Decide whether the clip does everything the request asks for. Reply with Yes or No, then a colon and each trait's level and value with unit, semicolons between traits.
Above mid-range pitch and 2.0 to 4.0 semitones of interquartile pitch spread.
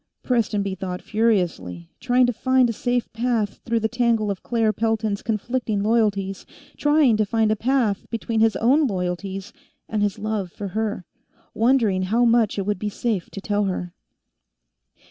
Yes: high, 215 Hz; average, 2.9 semitones